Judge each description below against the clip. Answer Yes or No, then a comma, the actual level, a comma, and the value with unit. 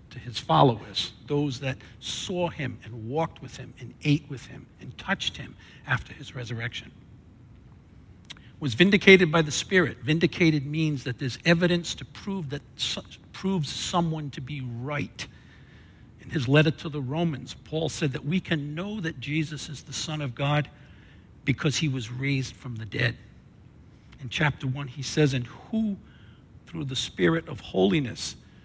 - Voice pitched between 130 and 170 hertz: Yes, medium, 140 Hz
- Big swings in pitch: No, average, 4.3 semitones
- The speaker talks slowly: No, average, 160 wpm